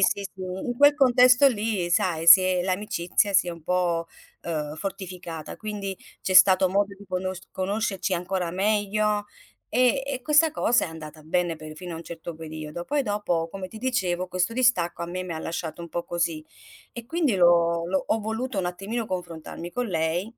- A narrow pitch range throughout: No, average, 3.8 semitones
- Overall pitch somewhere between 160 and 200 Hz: Yes, medium, 185 Hz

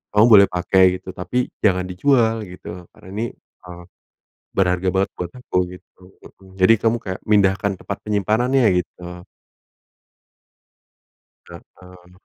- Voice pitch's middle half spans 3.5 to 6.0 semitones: No, average, 2.8 semitones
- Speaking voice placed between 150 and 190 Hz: No, very low, 95 Hz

